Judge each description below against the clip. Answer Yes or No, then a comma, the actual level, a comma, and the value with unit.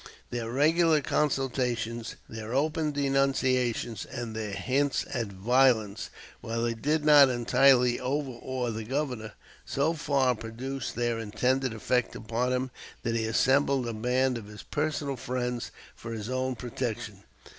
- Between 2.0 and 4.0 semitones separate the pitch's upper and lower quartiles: Yes, average, 3.0 semitones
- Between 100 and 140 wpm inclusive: Yes, slow, 135 wpm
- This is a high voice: No, low, 125 Hz